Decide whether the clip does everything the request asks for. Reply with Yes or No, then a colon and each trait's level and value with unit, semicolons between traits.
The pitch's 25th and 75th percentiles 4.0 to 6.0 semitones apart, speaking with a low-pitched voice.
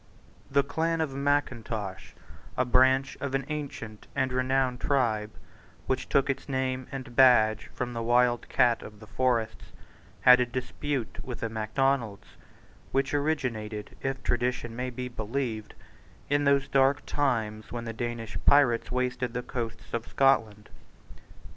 No: average, 2.9 semitones; low, 125 Hz